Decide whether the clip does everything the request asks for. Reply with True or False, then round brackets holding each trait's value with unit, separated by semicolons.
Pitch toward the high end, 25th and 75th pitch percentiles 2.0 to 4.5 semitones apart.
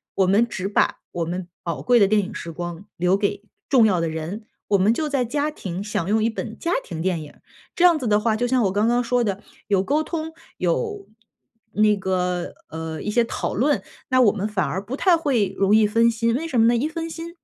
False (215 Hz; 4.9 semitones)